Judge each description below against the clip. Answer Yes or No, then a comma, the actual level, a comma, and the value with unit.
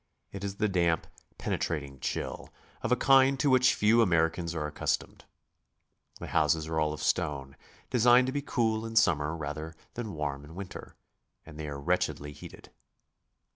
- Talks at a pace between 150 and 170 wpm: Yes, average, 165 wpm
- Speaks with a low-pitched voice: Yes, very low, 85 Hz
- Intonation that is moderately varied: No, wide, 7.1 semitones